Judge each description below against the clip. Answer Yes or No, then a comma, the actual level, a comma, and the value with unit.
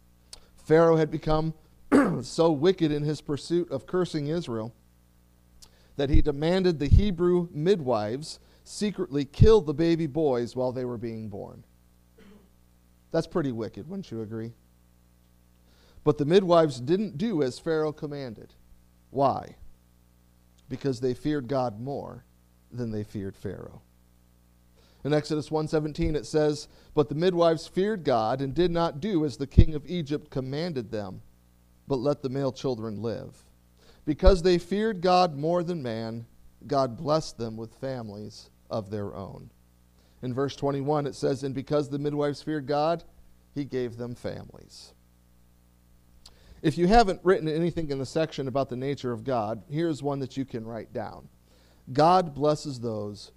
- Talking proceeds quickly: No, average, 145 wpm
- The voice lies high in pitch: No, low, 135 Hz